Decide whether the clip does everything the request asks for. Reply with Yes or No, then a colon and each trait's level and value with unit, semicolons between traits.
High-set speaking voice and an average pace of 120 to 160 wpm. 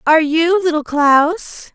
Yes: very high, 320 Hz; slow, 135 wpm